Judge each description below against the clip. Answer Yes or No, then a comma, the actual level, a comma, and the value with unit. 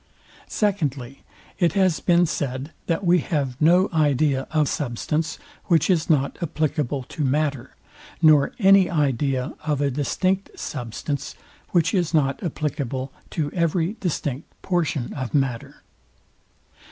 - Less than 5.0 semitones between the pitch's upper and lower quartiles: Yes, average, 3.9 semitones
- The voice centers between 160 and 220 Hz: No, medium, 150 Hz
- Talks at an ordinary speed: No, slow, 125 wpm